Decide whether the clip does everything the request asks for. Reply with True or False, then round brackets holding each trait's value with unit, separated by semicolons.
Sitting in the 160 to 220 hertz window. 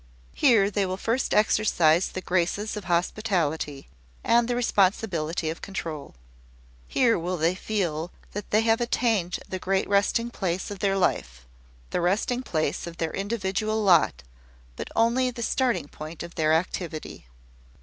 True (190 Hz)